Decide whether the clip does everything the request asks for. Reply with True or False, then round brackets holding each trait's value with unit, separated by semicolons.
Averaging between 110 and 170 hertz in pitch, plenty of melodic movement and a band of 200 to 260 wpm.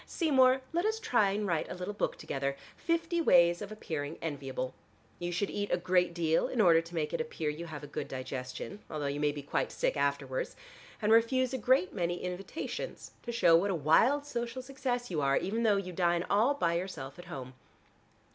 False (180 Hz; 7.3 semitones; 205 wpm)